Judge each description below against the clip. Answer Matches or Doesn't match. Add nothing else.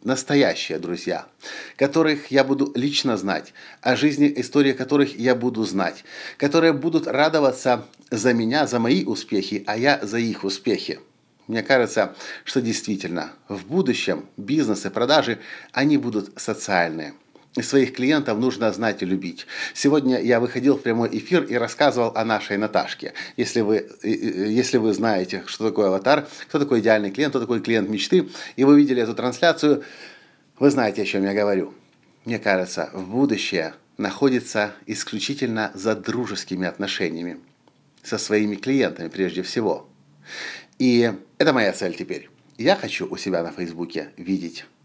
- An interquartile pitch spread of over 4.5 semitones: Matches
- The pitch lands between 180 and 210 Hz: Doesn't match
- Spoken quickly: Doesn't match